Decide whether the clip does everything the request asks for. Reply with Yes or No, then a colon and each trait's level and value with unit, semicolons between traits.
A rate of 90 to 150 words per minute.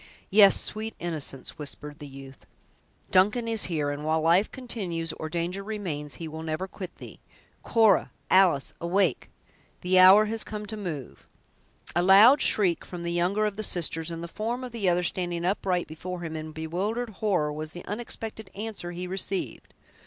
No: average, 175 wpm